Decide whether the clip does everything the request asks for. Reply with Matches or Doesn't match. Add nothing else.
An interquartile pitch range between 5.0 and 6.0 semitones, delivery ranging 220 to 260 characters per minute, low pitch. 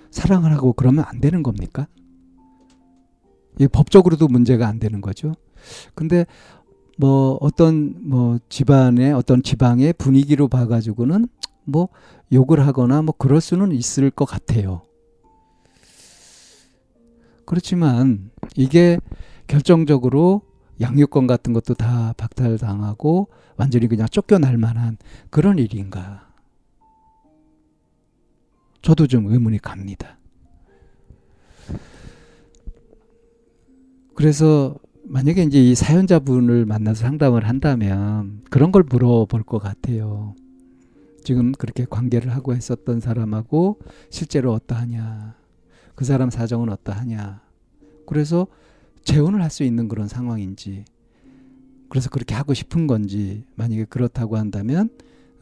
Matches